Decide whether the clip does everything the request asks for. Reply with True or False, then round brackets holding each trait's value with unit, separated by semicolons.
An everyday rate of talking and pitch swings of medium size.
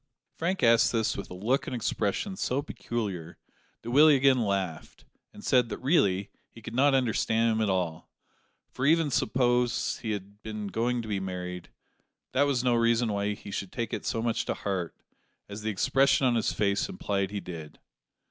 True (185 wpm; 4.1 semitones)